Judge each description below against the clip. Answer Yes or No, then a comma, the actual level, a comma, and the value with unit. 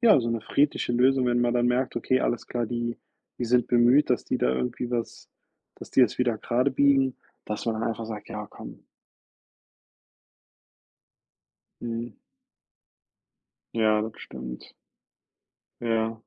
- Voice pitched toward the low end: Yes, low, 120 Hz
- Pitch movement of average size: No, narrow, 1.9 semitones